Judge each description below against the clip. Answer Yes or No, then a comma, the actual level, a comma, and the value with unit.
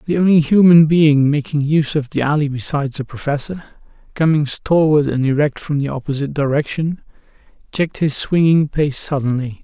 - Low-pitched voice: No, medium, 150 Hz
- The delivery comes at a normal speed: Yes, average, 155 wpm